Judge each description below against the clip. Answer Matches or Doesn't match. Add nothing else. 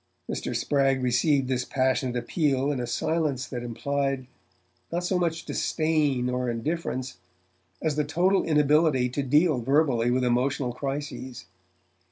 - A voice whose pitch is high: Doesn't match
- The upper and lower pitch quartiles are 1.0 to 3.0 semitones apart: Doesn't match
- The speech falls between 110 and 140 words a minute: Matches